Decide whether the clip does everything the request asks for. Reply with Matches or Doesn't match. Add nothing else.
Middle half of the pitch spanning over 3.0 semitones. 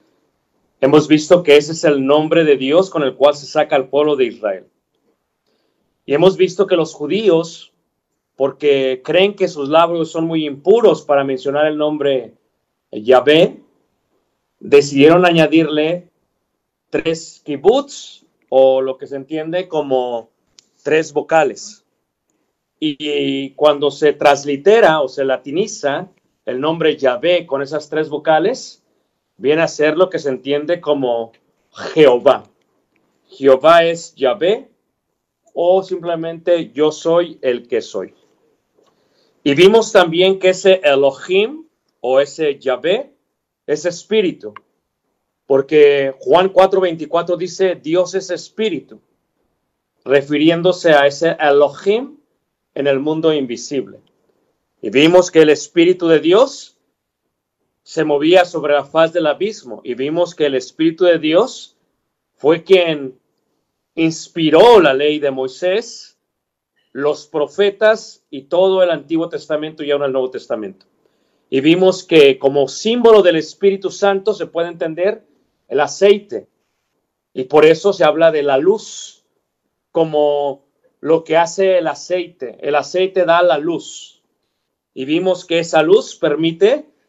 Matches